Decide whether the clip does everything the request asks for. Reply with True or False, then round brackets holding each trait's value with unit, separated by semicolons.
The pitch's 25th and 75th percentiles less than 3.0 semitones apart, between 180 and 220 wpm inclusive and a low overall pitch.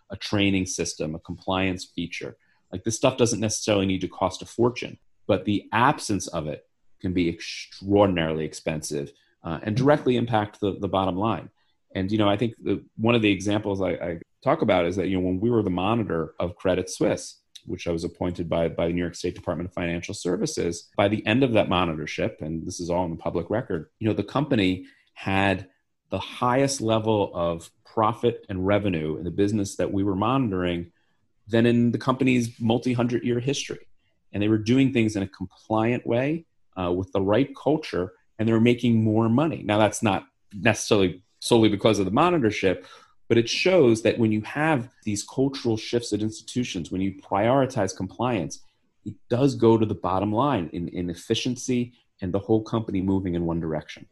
False (4.1 semitones; 195 wpm; 100 Hz)